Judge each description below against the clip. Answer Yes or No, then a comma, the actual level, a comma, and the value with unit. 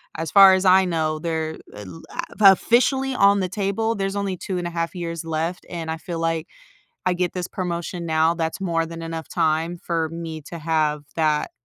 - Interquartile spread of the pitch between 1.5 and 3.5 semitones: Yes, narrow, 2.4 semitones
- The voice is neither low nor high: Yes, medium, 170 Hz